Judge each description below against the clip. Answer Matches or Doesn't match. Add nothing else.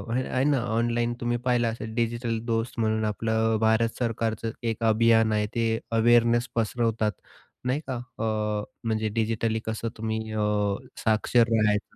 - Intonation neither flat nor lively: Doesn't match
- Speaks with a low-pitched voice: Matches